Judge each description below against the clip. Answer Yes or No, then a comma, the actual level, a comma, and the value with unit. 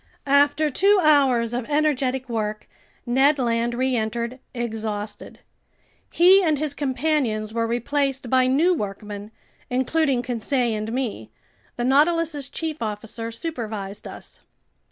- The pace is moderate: No, slow, 115 wpm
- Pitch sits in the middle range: No, very high, 255 Hz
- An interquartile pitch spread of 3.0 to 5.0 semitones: Yes, average, 4.3 semitones